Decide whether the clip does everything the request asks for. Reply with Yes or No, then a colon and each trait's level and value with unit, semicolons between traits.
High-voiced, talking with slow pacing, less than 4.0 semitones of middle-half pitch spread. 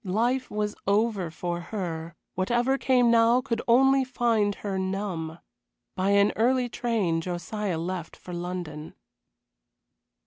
No: high, 205 Hz; slow, 125 wpm; average, 5.0 semitones